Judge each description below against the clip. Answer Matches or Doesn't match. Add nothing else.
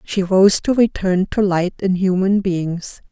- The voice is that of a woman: Matches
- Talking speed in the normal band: Matches